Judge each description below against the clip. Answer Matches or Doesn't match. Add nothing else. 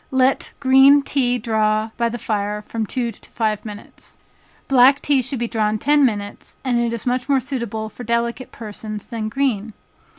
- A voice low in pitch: Doesn't match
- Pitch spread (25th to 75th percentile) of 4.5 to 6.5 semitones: Doesn't match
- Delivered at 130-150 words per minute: Doesn't match